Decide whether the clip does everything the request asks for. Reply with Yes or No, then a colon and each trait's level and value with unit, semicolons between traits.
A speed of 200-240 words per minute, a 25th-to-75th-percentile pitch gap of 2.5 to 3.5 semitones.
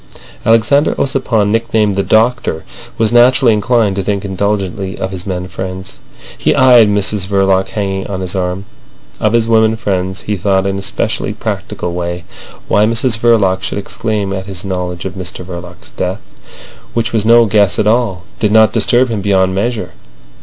No: average, 170 wpm; average, 3.1 semitones